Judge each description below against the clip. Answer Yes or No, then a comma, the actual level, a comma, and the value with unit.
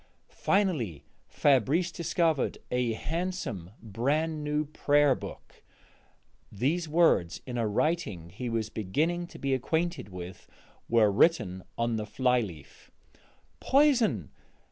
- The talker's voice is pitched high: No, low, 130 Hz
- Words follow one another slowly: Yes, slow, 115 wpm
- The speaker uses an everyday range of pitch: No, wide, 7.5 semitones